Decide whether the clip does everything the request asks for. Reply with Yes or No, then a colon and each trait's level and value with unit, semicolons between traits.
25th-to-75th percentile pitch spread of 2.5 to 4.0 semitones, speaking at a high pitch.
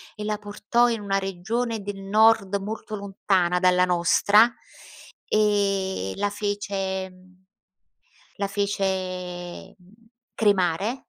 No: narrow, 1.9 semitones; high, 200 Hz